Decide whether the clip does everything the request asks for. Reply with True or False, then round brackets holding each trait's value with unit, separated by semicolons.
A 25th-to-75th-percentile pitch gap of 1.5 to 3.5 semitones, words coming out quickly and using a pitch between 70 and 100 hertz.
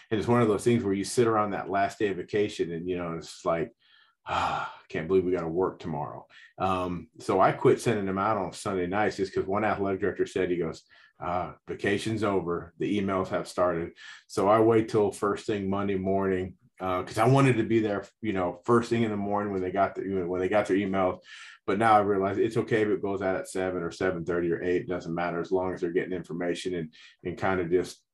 True (2.4 semitones; 245 wpm; 95 Hz)